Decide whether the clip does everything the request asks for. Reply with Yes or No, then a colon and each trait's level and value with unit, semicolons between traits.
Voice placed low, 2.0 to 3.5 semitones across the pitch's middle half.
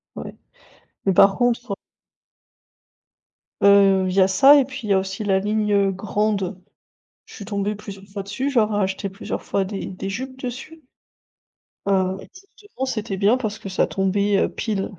No: high, 200 Hz; narrow, 2.5 semitones